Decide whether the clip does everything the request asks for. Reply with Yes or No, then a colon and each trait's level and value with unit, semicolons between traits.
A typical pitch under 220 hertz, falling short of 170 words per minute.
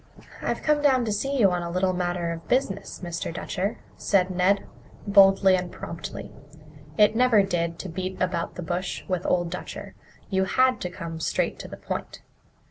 No: medium, 185 Hz; average, 180 wpm